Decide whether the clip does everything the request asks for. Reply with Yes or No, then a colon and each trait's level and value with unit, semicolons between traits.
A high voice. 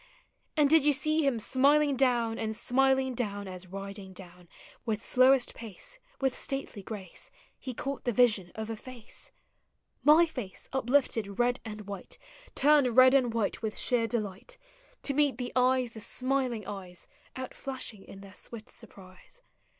Yes: high, 240 Hz